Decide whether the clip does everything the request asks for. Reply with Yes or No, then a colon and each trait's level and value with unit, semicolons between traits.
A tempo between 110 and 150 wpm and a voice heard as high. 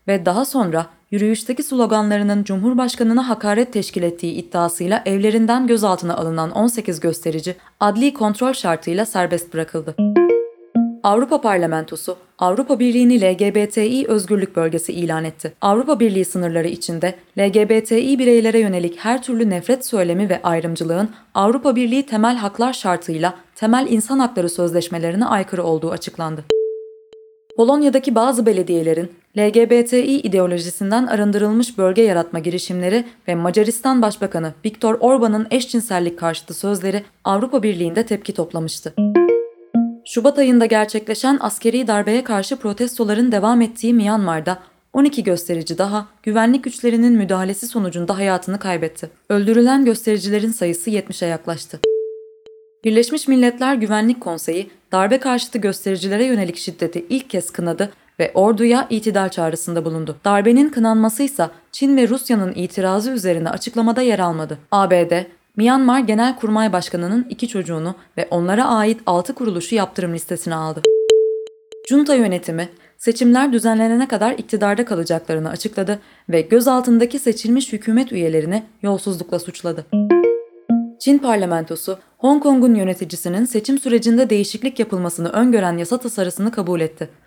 Yes: average, 115 wpm; high, 210 Hz